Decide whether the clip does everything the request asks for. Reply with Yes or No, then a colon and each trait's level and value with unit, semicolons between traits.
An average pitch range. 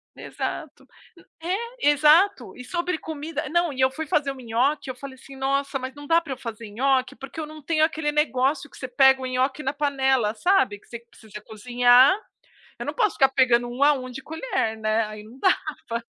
Yes: average, 3.5 semitones